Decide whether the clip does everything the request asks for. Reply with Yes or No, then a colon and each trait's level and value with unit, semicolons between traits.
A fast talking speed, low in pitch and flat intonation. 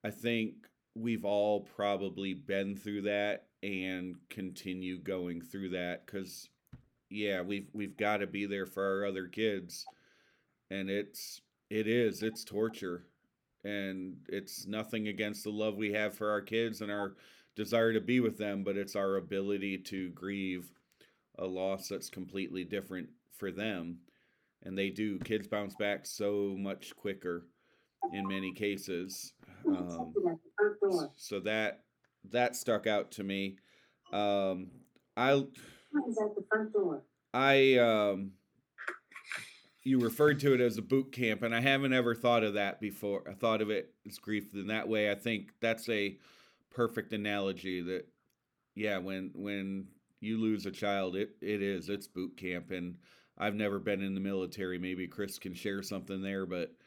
No: average, 155 wpm; low, 100 Hz; narrow, 2.2 semitones